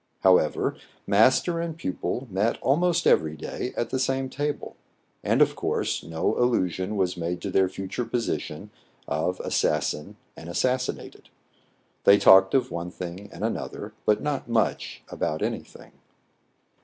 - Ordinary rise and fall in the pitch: No, wide, 6.3 semitones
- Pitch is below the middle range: Yes, low, 100 Hz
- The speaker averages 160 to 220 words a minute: No, average, 145 wpm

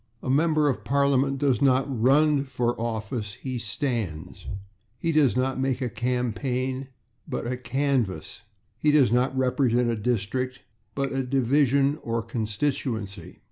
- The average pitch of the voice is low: Yes, low, 130 Hz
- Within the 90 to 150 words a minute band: Yes, average, 140 wpm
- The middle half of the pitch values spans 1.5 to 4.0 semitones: Yes, average, 2.8 semitones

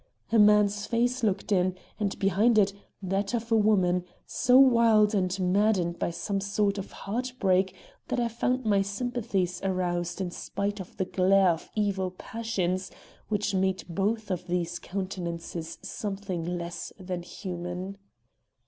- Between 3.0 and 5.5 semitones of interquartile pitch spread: No, narrow, 2.6 semitones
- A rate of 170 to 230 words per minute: No, average, 150 wpm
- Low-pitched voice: No, high, 195 Hz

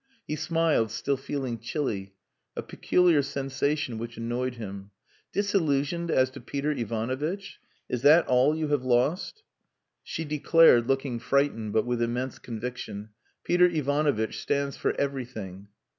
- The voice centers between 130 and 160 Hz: Yes, low, 135 Hz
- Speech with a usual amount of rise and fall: Yes, average, 4.2 semitones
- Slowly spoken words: Yes, slow, 130 wpm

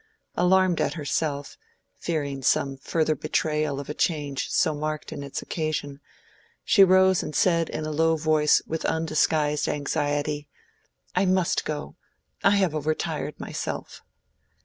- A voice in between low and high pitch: Yes, medium, 155 Hz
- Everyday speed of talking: No, slow, 130 wpm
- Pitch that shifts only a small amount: Yes, narrow, 1.9 semitones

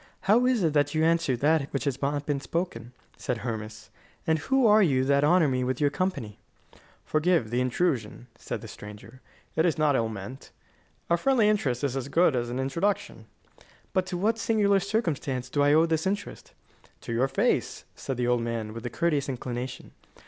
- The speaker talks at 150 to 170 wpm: No, average, 190 wpm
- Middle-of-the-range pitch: Yes, medium, 145 Hz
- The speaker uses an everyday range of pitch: No, wide, 5.9 semitones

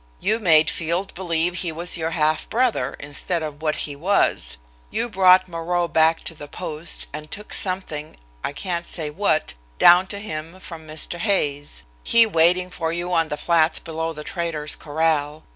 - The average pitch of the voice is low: No, medium, 165 Hz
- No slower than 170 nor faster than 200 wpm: Yes, average, 175 wpm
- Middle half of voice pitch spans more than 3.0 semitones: No, average, 2.7 semitones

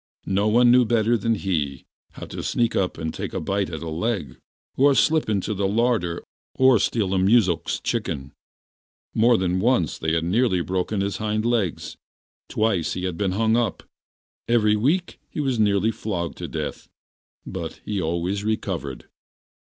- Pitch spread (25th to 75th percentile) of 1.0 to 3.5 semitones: No, average, 4.5 semitones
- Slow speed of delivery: No, average, 170 wpm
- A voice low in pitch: Yes, low, 100 Hz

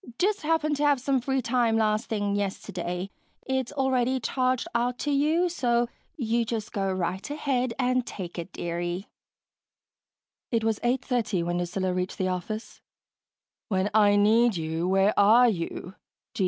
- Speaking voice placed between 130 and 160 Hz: No, high, 225 Hz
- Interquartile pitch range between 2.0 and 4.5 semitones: No, average, 5.1 semitones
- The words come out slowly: No, average, 150 wpm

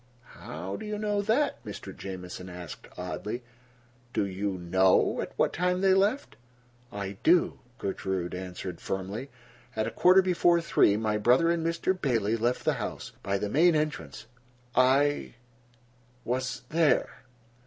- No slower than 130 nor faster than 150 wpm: Yes, slow, 135 wpm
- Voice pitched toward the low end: Yes, low, 120 Hz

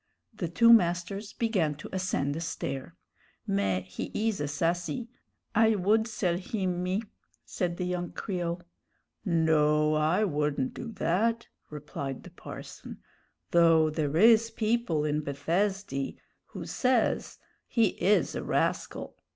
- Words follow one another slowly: Yes, slow, 130 wpm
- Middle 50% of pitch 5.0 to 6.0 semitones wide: Yes, wide, 5.6 semitones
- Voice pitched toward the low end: No, medium, 175 Hz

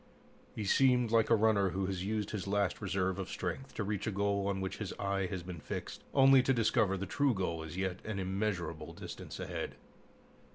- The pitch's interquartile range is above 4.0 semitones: No, average, 2.8 semitones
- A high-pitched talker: No, low, 100 Hz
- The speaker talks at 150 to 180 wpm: No, fast, 205 wpm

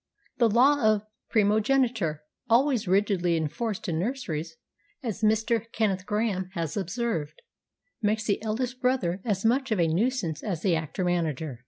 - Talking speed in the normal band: Yes, average, 145 wpm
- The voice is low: No, high, 210 Hz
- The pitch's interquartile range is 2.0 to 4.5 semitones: No, average, 5.2 semitones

